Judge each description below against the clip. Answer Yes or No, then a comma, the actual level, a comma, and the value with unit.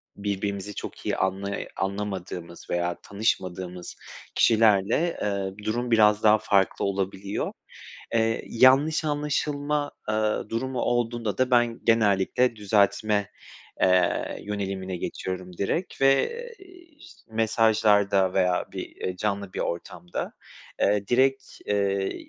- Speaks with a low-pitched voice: Yes, low, 105 Hz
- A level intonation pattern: No, average, 3.5 semitones